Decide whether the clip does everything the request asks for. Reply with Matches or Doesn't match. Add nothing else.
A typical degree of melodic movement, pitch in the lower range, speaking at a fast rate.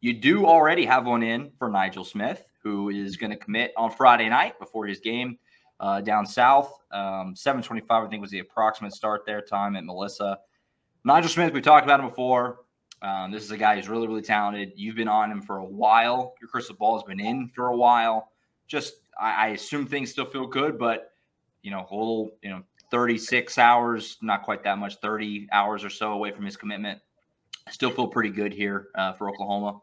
Matches